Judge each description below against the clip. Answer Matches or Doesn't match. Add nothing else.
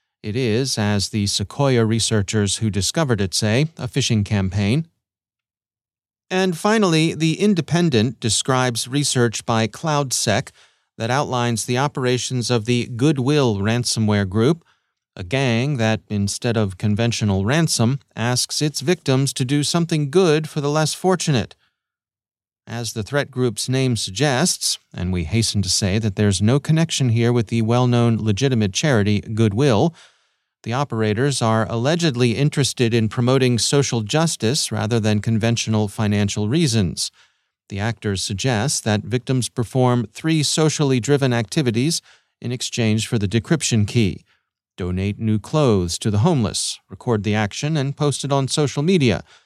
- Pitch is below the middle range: Matches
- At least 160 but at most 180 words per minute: Doesn't match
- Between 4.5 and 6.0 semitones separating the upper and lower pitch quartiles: Matches